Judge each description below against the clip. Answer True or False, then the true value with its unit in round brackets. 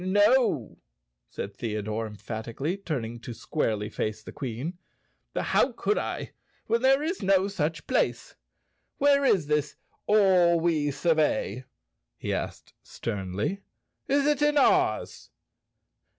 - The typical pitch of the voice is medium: True (160 Hz)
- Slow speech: True (120 wpm)